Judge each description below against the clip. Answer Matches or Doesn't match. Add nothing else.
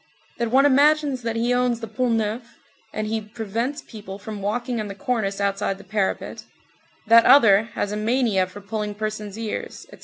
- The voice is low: Doesn't match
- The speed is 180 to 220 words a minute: Matches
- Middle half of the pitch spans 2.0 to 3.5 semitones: Matches